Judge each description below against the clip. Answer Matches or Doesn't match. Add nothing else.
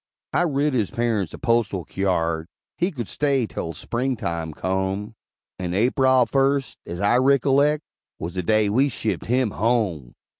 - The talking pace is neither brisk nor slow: Matches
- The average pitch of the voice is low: Matches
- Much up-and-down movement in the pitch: Matches